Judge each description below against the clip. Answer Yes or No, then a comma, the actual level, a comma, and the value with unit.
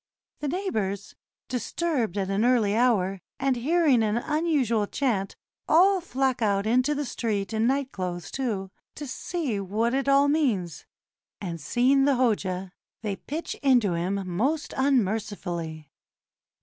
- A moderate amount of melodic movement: No, wide, 5.8 semitones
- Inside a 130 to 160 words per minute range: Yes, average, 145 wpm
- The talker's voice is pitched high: Yes, high, 235 Hz